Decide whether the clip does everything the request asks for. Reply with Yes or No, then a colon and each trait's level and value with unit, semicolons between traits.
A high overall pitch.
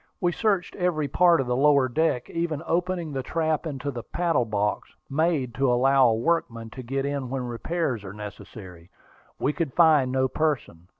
No: low, 135 Hz